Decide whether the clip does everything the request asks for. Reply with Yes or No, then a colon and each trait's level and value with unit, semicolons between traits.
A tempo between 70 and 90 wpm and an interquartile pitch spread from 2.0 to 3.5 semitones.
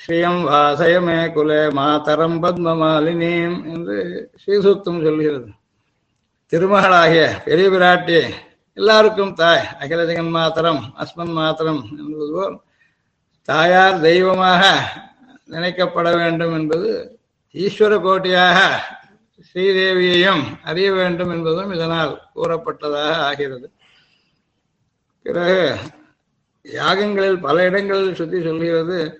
Yes: average, 80 wpm; average, 2.8 semitones